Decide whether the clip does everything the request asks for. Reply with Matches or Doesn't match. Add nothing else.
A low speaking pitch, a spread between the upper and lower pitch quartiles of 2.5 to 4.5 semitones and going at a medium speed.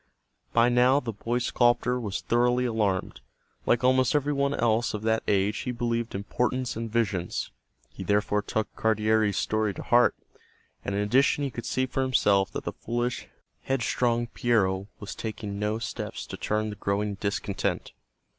Matches